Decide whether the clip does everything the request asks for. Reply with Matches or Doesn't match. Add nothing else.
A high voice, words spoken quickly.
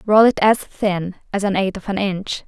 Matches